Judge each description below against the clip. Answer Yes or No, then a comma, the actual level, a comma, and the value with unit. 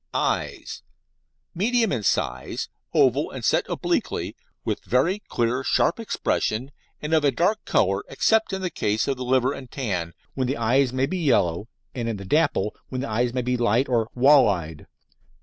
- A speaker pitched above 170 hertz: No, low, 125 Hz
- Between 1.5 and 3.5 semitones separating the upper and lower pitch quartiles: No, average, 4.6 semitones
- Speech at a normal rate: Yes, average, 180 wpm